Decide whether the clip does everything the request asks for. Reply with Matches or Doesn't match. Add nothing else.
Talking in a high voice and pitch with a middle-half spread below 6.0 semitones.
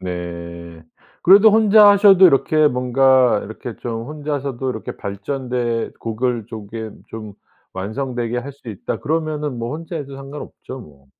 Doesn't match